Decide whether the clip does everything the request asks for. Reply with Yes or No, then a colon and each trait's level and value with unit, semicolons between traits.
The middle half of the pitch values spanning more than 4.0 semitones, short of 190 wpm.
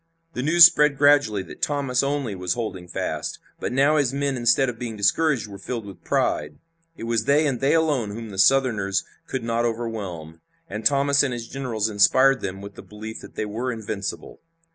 No: average, 4.8 semitones; average, 195 wpm